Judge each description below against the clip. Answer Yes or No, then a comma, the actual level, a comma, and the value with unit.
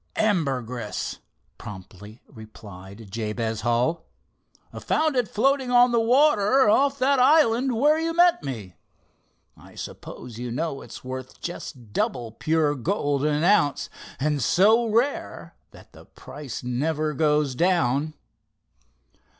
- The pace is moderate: No, slow, 120 wpm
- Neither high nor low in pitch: Yes, medium, 150 Hz